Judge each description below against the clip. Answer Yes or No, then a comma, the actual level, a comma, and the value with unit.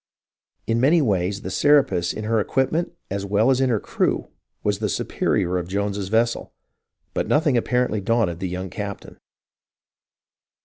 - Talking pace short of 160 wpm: Yes, average, 150 wpm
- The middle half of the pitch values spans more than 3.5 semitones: Yes, average, 4.4 semitones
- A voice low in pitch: Yes, low, 105 Hz